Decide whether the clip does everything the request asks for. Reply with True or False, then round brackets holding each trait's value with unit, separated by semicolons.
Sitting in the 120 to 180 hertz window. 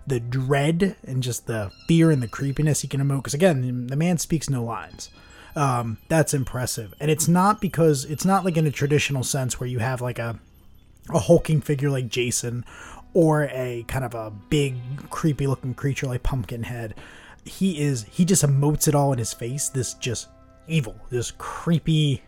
True (140 Hz)